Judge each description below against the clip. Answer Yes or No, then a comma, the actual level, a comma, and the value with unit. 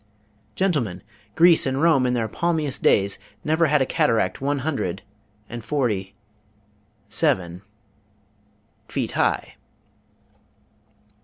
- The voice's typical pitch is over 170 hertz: No, low, 130 Hz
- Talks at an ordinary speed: No, slow, 100 wpm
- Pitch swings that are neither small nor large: No, wide, 7.2 semitones